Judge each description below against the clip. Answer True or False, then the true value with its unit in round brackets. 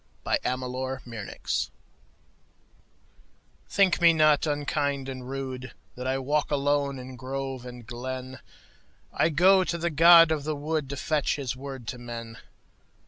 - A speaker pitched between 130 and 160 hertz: True (135 Hz)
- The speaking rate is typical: False (125 wpm)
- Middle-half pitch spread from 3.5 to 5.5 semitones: False (3.0 semitones)